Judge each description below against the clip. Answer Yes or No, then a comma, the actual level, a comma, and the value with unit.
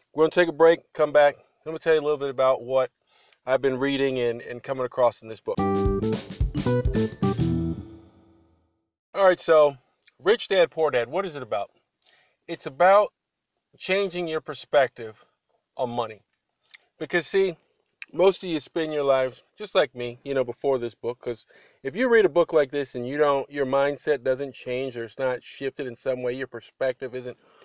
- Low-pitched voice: Yes, low, 130 Hz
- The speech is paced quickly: No, average, 185 wpm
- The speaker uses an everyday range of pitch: Yes, average, 4.4 semitones